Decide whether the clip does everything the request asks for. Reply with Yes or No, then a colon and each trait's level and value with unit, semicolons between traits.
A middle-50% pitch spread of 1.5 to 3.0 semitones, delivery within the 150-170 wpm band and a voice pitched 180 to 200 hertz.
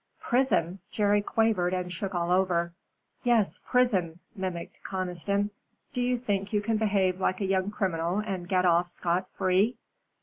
Yes: average, 2.7 semitones; average, 155 wpm; high, 190 Hz